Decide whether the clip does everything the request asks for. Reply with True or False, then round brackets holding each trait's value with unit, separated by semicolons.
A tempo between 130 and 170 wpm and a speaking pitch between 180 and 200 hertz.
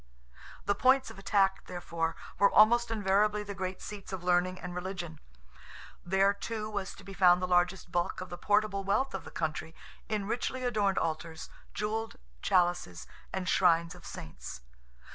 True (160 wpm; 190 Hz)